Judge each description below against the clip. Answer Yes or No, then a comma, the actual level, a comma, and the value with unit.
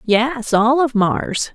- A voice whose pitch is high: Yes, high, 240 Hz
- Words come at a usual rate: Yes, average, 155 wpm